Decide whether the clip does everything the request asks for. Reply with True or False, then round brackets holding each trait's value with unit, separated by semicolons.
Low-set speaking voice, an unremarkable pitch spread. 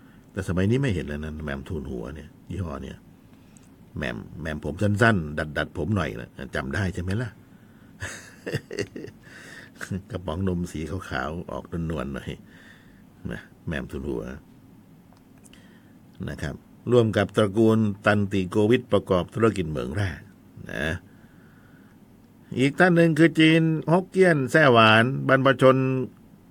False (105 Hz; 6.4 semitones)